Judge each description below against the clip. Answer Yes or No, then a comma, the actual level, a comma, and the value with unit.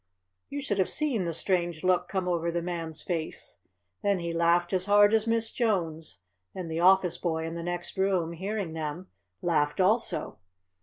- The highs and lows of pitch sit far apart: No, average, 2.9 semitones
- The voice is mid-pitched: Yes, medium, 175 Hz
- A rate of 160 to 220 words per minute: Yes, average, 175 wpm